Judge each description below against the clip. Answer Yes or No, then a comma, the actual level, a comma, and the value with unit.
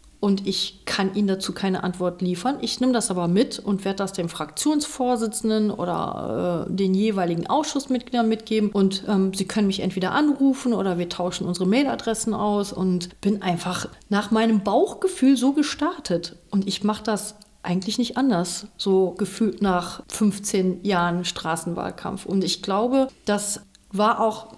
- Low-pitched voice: No, high, 200 Hz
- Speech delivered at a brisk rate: No, average, 155 wpm